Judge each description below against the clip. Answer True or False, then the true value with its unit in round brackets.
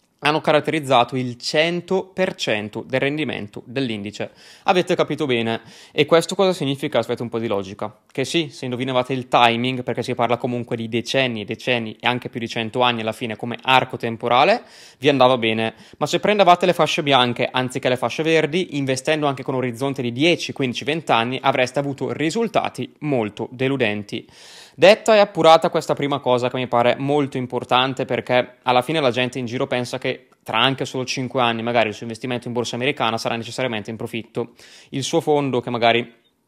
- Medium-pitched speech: False (125 Hz)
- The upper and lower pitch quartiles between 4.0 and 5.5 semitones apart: False (3.6 semitones)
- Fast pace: True (185 wpm)